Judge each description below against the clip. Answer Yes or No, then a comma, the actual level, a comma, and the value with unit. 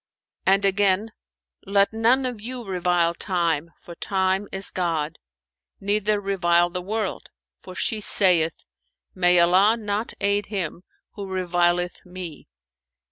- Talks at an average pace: No, slow, 125 wpm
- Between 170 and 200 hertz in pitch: Yes, high, 190 Hz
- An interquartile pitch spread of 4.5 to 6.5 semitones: No, average, 2.7 semitones